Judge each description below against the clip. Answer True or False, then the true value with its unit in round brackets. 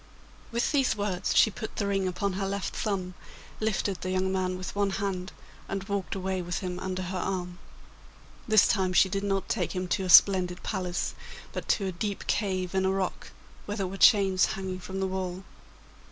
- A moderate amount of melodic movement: False (1.3 semitones)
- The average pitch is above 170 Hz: True (190 Hz)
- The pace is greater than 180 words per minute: True (195 wpm)